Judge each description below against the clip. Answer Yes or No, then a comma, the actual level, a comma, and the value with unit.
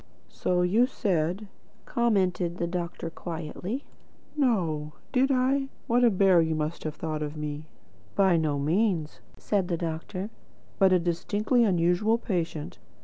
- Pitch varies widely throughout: No, average, 4.8 semitones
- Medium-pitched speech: Yes, medium, 180 Hz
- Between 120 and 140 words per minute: Yes, slow, 135 wpm